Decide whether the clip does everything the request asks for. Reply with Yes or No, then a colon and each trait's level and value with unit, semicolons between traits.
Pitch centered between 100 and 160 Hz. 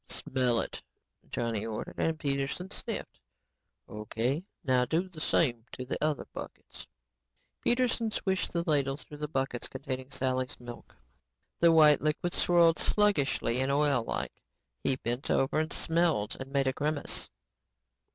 Yes: medium, 140 Hz